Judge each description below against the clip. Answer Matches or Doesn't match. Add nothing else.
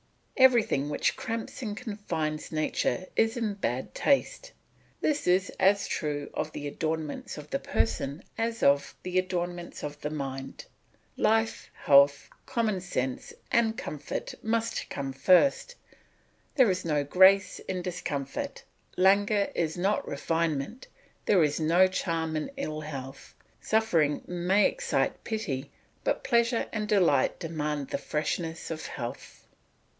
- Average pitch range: Doesn't match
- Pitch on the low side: Doesn't match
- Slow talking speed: Matches